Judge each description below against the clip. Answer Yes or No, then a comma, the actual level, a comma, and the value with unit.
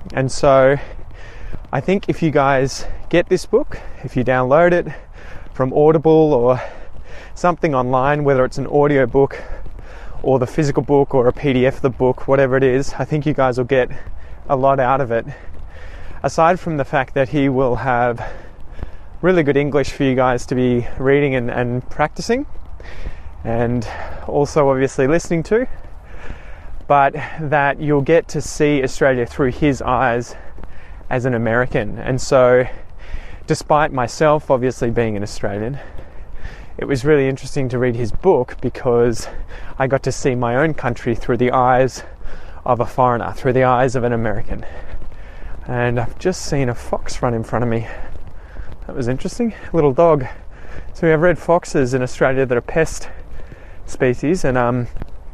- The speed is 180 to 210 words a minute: No, average, 165 wpm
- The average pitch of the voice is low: Yes, low, 130 Hz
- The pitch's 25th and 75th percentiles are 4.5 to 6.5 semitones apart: No, average, 3.7 semitones